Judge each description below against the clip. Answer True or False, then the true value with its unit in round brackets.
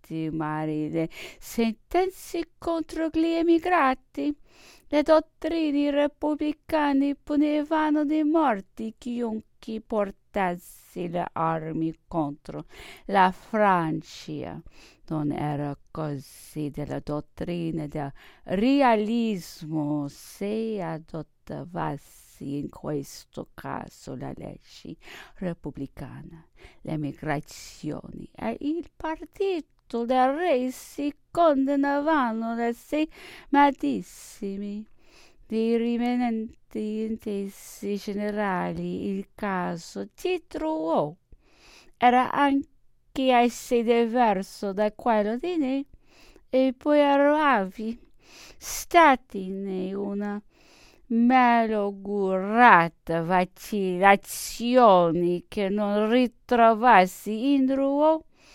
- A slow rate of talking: True (75 wpm)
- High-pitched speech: True (225 Hz)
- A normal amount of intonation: False (8.2 semitones)